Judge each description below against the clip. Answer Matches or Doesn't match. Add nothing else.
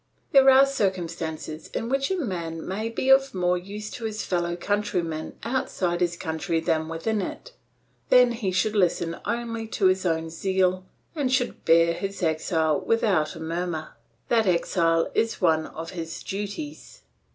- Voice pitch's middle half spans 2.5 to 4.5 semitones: Doesn't match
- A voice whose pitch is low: Doesn't match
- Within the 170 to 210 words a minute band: Doesn't match